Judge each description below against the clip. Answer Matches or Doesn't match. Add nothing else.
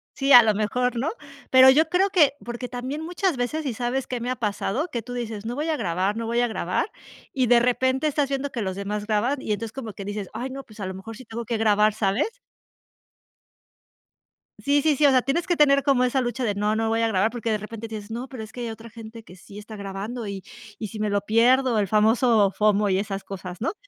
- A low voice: Doesn't match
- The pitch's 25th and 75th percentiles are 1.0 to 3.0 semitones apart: Doesn't match